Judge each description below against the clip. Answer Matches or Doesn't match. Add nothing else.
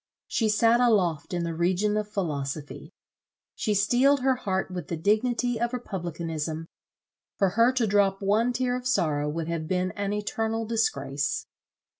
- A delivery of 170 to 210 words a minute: Doesn't match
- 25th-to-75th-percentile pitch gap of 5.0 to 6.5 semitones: Matches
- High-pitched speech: Matches